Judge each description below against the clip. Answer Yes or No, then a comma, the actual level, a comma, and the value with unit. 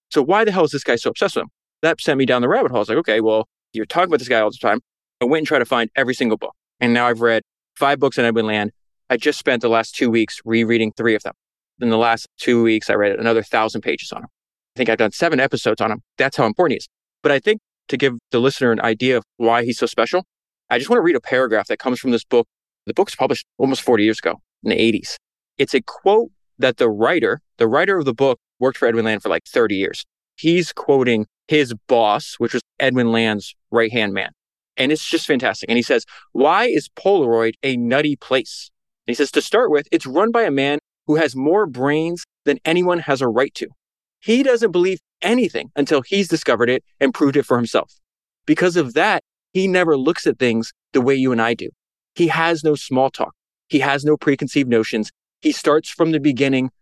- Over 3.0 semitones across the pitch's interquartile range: Yes, average, 4.9 semitones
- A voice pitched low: Yes, low, 130 Hz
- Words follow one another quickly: Yes, fast, 240 wpm